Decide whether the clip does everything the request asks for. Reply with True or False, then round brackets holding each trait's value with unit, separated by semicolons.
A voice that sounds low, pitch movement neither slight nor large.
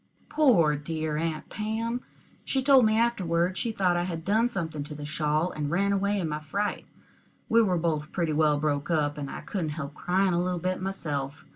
False (170 Hz; 4.7 semitones)